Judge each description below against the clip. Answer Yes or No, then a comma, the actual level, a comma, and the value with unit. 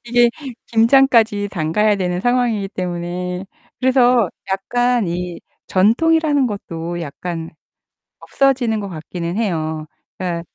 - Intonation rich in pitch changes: Yes, wide, 5.7 semitones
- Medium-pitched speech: No, high, 200 Hz